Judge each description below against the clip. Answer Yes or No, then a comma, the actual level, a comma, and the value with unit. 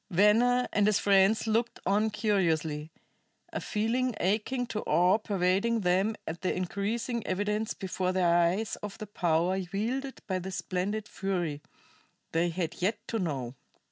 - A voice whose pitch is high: Yes, high, 195 Hz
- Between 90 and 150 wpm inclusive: Yes, average, 145 wpm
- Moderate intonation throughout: Yes, average, 3.3 semitones